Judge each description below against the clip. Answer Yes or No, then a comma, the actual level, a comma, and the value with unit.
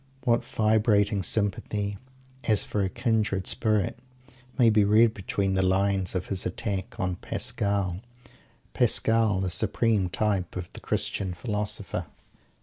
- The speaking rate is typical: No, slow, 130 wpm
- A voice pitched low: Yes, low, 100 Hz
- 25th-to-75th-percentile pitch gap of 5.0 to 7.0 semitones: No, narrow, 2.4 semitones